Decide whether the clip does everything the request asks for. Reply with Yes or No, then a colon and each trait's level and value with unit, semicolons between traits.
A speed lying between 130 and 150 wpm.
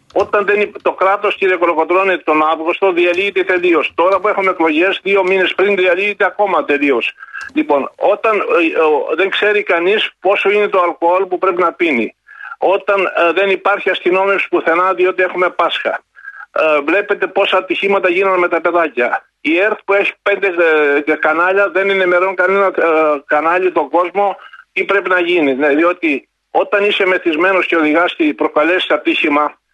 No: average, 165 wpm